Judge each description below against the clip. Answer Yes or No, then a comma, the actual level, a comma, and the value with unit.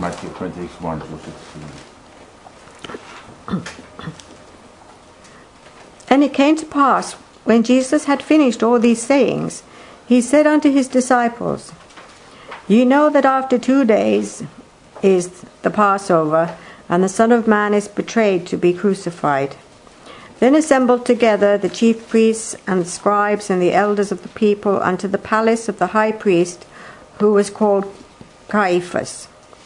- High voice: Yes, high, 210 Hz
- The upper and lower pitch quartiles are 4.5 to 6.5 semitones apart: Yes, average, 5.2 semitones